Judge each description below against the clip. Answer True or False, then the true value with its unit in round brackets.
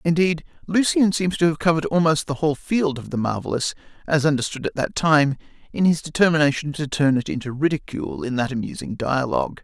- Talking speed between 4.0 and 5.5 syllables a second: False (6.0 syllables/s)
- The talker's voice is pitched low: False (150 Hz)